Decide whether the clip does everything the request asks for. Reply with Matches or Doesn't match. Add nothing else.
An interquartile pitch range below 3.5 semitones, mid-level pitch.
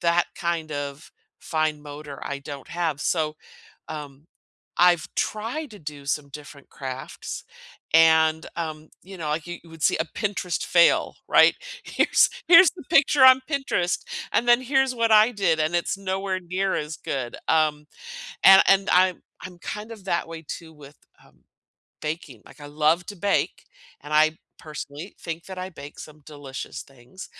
Doesn't match